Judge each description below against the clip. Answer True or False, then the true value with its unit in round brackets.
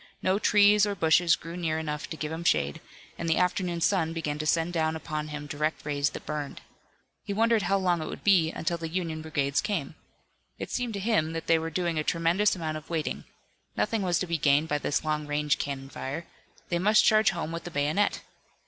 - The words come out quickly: True (220 wpm)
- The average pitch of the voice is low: False (165 Hz)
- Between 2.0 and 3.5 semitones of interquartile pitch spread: True (2.9 semitones)